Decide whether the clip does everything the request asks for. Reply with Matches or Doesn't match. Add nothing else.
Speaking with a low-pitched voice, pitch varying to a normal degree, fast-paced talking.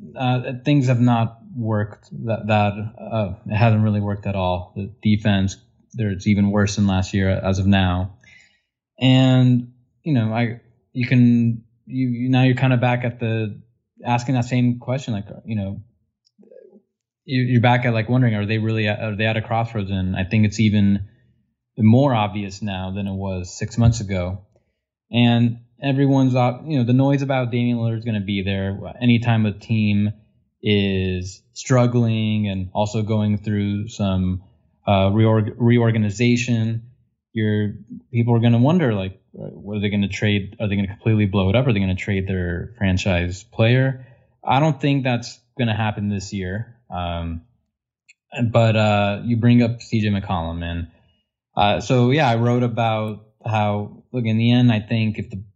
Doesn't match